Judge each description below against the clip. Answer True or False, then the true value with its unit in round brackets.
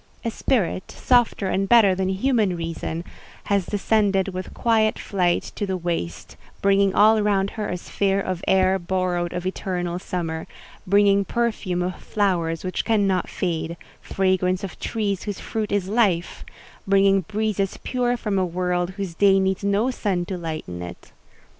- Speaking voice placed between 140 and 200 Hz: True (190 Hz)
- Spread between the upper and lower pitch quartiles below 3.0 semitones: True (2.4 semitones)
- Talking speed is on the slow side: False (150 wpm)